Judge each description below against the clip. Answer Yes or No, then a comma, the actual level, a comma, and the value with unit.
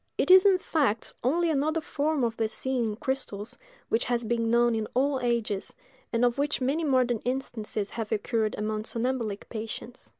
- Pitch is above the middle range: Yes, high, 240 Hz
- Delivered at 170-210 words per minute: Yes, average, 175 wpm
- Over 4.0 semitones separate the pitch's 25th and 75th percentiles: No, average, 3.5 semitones